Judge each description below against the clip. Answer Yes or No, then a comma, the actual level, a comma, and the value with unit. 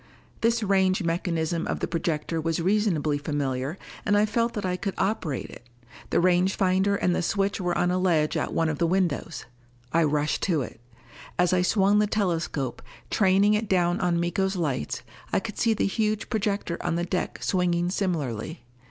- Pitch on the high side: No, medium, 180 Hz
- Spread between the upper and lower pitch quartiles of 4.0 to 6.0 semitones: No, average, 3.3 semitones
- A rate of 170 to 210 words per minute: Yes, average, 185 wpm